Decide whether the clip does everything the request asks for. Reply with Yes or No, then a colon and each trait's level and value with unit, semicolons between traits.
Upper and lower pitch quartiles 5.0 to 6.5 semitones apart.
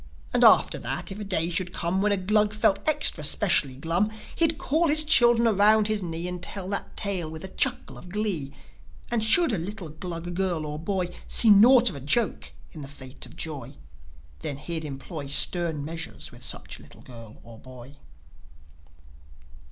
Yes: wide, 5.5 semitones